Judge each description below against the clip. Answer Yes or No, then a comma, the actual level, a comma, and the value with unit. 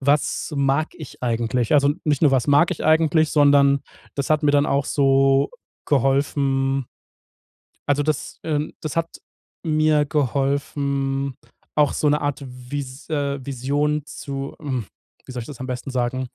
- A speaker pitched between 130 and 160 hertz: Yes, medium, 140 Hz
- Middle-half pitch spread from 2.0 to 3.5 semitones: No, narrow, 1.6 semitones